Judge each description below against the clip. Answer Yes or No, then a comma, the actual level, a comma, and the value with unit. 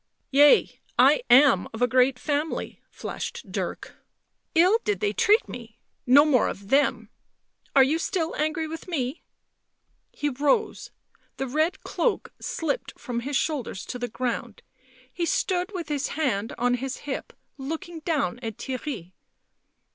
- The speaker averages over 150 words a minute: No, average, 145 wpm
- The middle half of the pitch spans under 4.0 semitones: No, average, 4.7 semitones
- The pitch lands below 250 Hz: No, very high, 285 Hz